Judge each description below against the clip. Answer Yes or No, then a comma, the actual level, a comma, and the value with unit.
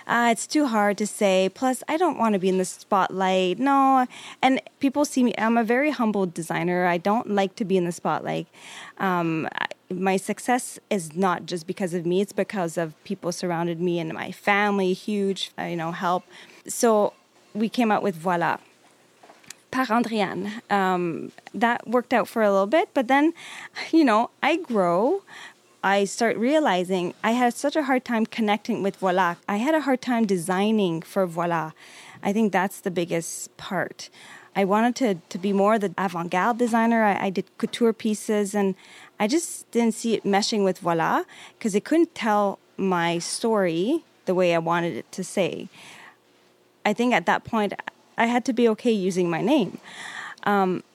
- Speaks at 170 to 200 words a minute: Yes, average, 180 wpm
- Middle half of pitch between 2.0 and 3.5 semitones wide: No, average, 4.3 semitones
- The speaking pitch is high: Yes, high, 200 Hz